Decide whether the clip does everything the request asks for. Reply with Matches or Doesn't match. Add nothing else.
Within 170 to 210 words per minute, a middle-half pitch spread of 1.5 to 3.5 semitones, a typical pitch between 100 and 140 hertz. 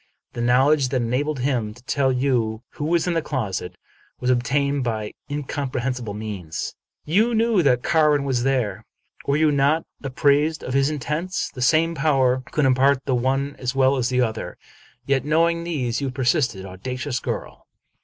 Matches